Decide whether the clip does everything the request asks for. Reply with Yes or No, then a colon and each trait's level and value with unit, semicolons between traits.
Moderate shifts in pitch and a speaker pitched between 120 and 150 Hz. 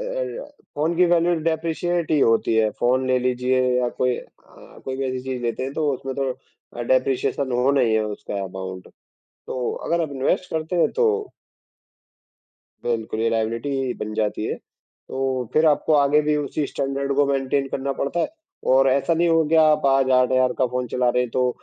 Yes: average, 3.9 semitones; low, 135 Hz